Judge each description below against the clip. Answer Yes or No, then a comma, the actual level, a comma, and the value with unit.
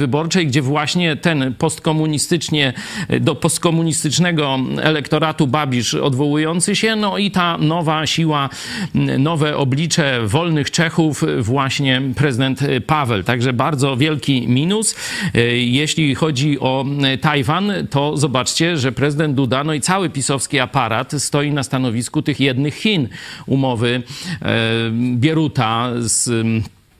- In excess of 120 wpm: No, average, 115 wpm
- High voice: No, medium, 145 Hz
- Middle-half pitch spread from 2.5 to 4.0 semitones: Yes, average, 3.3 semitones